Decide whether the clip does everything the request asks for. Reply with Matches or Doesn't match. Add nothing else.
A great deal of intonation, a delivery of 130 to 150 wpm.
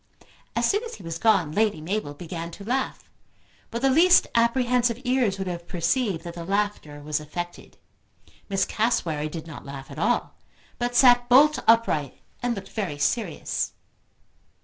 Doesn't match